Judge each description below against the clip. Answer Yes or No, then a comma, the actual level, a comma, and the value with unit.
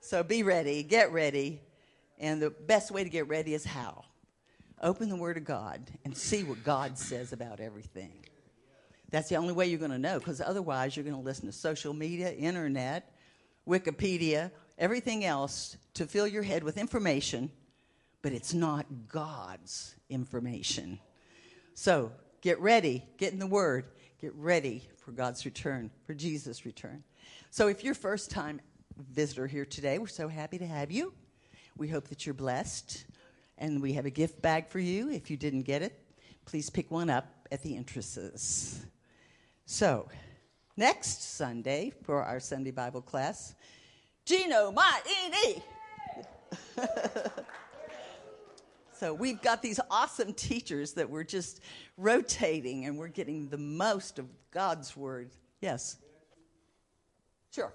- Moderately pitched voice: Yes, medium, 150 Hz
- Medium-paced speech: Yes, average, 150 wpm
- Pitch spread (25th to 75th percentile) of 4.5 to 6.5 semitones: Yes, average, 5.1 semitones